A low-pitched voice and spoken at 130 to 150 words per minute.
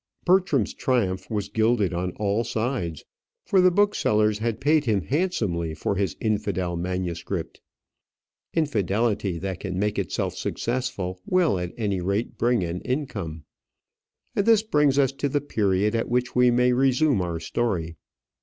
Yes: low, 110 Hz; average, 145 wpm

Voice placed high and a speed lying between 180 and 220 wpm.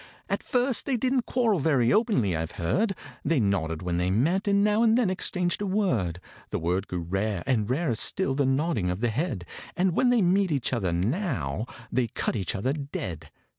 No: low, 135 Hz; average, 200 wpm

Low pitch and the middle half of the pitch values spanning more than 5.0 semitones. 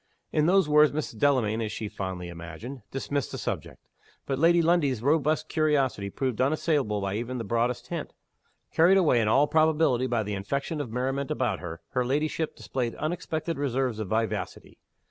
Yes: low, 130 Hz; wide, 5.5 semitones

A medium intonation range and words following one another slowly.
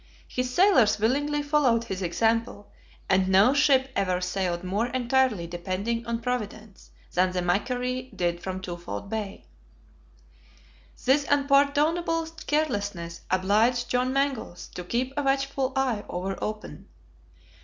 No: wide, 6.0 semitones; slow, 120 wpm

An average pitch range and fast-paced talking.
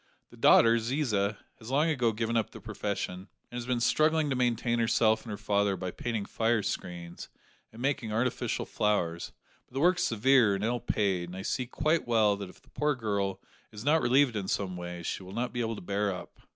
Yes: average, 3.7 semitones; fast, 215 wpm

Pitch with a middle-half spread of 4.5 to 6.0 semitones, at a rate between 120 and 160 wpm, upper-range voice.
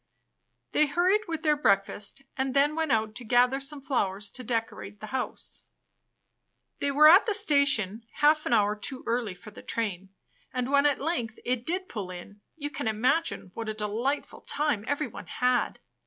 No: wide, 5.4 semitones; average, 175 wpm; very high, 250 Hz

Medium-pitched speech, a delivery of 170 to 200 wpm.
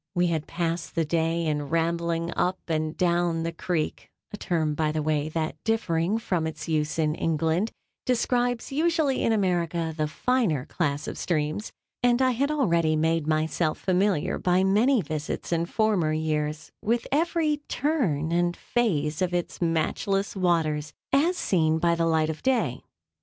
No: medium, 170 Hz; average, 160 wpm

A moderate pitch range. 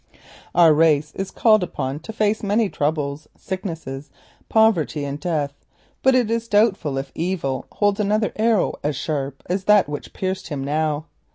No: wide, 6.1 semitones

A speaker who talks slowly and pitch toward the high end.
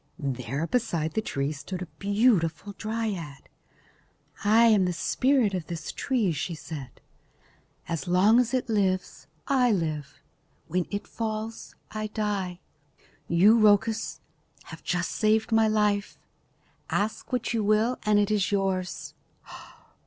Yes: slow, 130 wpm; high, 205 Hz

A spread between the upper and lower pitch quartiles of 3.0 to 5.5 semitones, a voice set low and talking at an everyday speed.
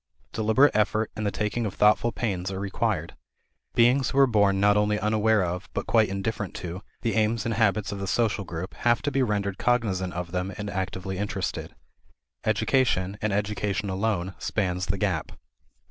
No: narrow, 2.5 semitones; low, 105 Hz; average, 175 wpm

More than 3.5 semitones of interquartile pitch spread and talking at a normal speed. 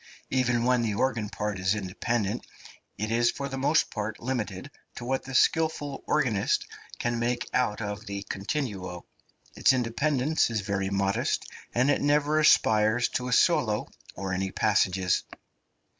Yes: average, 4.6 semitones; average, 150 wpm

